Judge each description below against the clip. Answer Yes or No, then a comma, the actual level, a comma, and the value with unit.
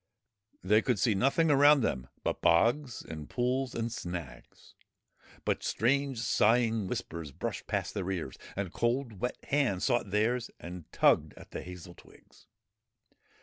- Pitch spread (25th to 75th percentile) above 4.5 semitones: Yes, wide, 5.6 semitones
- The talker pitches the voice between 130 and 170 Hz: No, low, 115 Hz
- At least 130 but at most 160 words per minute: Yes, average, 145 wpm